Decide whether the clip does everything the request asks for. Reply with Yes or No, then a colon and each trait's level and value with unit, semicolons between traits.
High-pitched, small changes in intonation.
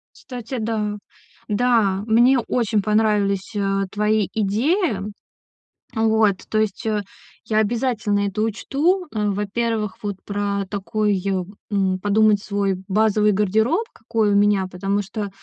Yes: high, 210 Hz; narrow, 1.8 semitones